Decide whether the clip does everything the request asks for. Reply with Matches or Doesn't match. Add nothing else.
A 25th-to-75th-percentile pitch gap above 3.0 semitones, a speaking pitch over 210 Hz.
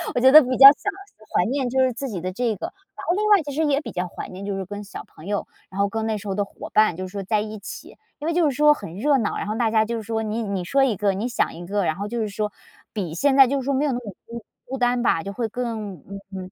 Matches